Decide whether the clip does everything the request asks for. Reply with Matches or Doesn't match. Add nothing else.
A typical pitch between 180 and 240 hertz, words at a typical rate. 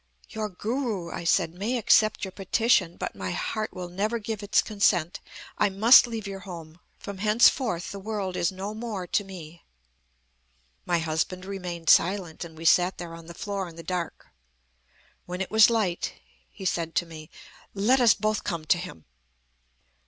Matches